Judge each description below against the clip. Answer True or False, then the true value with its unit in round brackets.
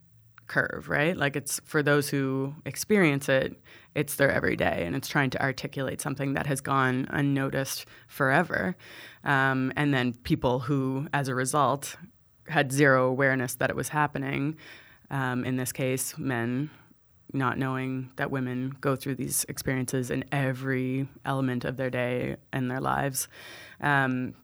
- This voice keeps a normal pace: True (150 wpm)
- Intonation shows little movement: True (1.6 semitones)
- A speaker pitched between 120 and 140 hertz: True (135 Hz)